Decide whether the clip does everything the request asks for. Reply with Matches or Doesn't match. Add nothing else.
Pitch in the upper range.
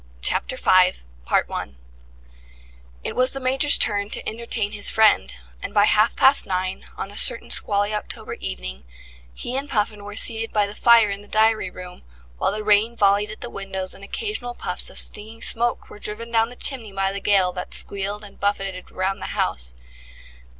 Matches